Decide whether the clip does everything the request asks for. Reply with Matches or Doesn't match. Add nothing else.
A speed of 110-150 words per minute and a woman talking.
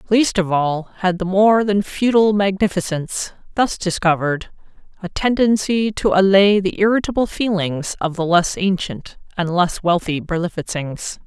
Matches